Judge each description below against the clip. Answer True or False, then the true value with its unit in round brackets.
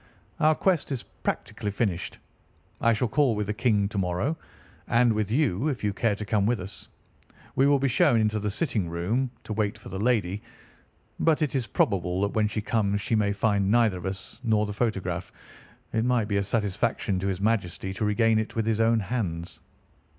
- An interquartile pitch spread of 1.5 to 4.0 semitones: True (2.9 semitones)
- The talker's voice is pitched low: True (105 Hz)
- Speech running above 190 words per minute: True (200 wpm)